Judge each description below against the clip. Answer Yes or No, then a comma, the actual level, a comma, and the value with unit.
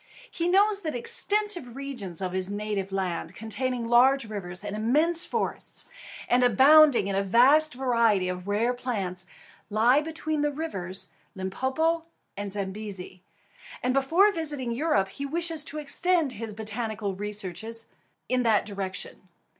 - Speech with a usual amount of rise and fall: No, wide, 6.9 semitones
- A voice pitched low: No, high, 235 Hz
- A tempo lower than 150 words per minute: Yes, average, 140 wpm